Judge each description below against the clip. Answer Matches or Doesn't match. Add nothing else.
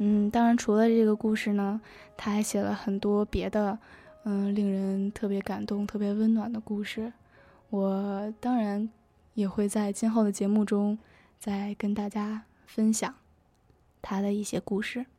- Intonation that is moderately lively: Doesn't match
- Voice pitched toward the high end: Matches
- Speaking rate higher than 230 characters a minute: Doesn't match